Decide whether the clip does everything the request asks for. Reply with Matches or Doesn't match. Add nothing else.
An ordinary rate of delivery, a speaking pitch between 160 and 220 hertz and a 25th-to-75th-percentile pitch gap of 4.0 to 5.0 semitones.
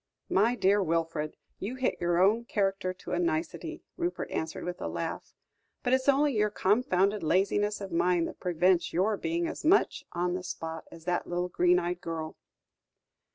Matches